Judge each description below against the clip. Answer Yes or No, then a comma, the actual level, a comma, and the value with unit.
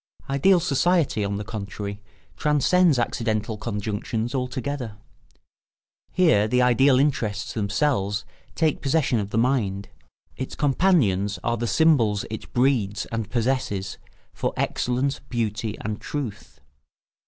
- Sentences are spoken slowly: Yes, slow, 115 wpm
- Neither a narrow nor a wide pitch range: Yes, average, 4.8 semitones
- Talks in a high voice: No, low, 120 Hz